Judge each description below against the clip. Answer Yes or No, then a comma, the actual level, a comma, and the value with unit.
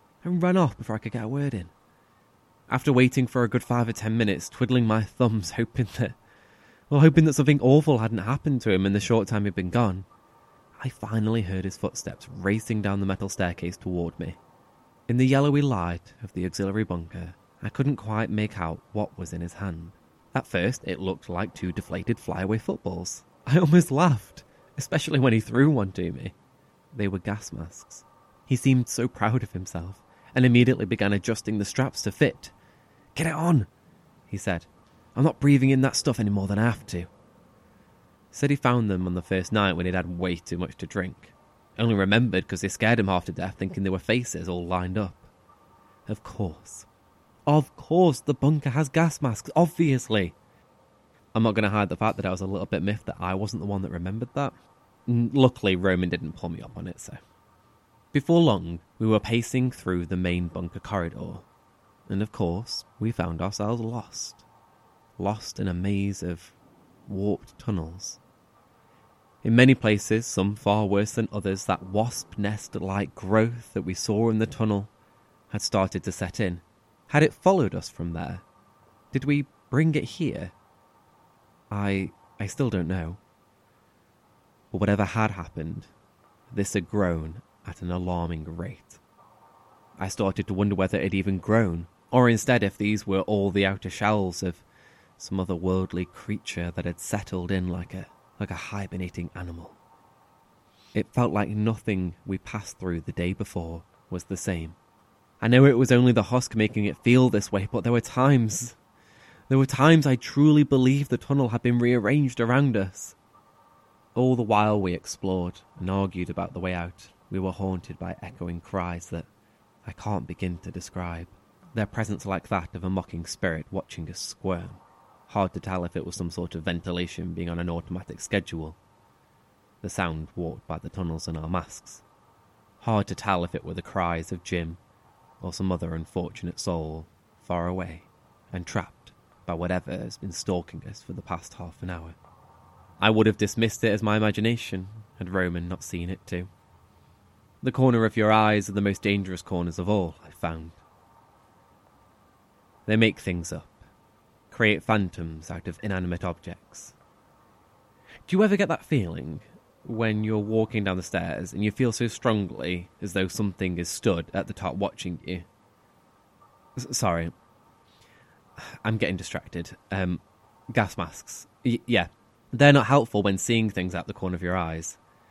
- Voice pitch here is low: Yes, low, 100 Hz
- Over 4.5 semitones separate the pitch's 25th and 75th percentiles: No, average, 4.1 semitones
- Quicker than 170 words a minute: Yes, average, 180 wpm